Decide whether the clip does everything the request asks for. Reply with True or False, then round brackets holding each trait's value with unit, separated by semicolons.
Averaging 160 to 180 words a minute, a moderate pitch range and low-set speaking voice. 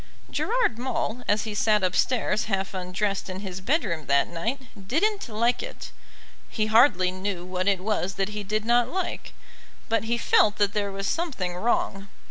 False (170 wpm; 3.8 semitones; 210 Hz)